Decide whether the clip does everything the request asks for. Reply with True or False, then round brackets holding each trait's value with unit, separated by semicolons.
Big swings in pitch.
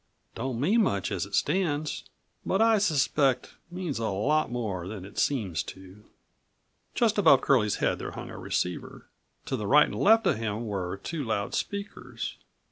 True (8.3 semitones)